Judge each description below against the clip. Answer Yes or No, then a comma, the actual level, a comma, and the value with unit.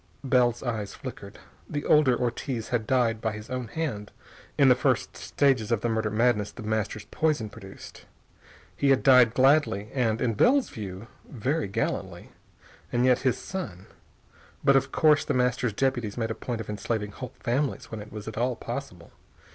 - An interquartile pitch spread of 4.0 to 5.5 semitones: No, average, 3.5 semitones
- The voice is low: Yes, low, 120 Hz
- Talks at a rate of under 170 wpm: No, average, 175 wpm